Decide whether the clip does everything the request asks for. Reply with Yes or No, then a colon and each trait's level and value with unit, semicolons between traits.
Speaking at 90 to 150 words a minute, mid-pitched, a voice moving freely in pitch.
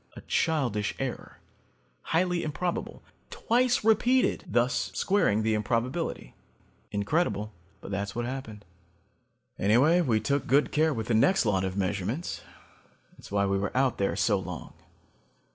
No: slow, 135 wpm; low, 120 Hz; wide, 8.0 semitones